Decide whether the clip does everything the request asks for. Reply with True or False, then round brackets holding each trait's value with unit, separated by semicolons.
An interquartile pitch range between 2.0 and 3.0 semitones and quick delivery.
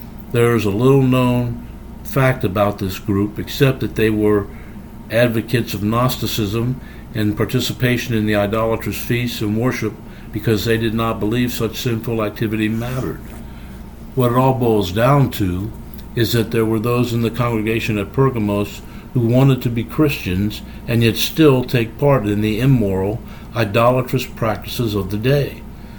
False (2.5 semitones; 155 wpm)